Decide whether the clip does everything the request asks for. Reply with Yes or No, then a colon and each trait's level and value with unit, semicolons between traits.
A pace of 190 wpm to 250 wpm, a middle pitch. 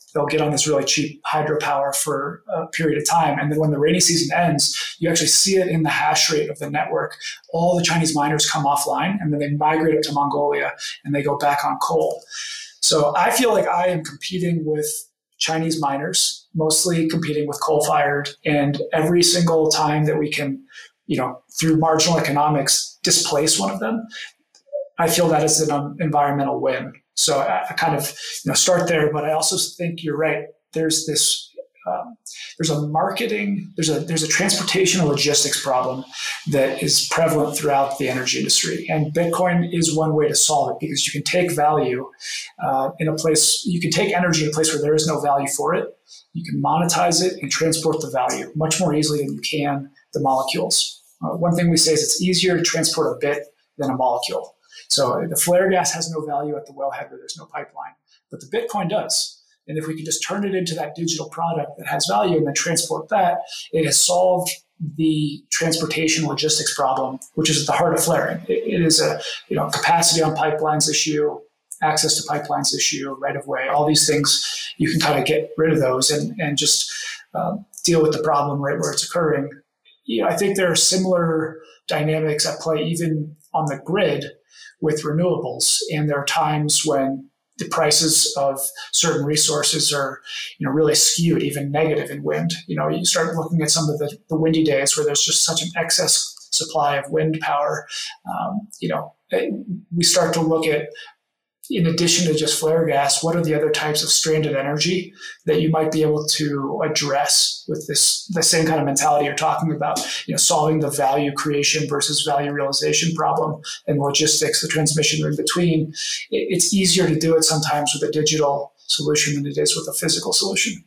Yes: average, 200 wpm; medium, 155 Hz